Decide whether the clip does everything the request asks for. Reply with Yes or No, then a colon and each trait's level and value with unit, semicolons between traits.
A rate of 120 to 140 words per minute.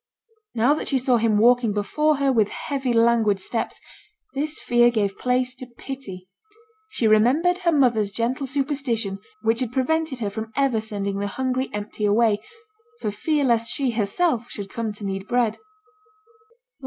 No: average, 160 wpm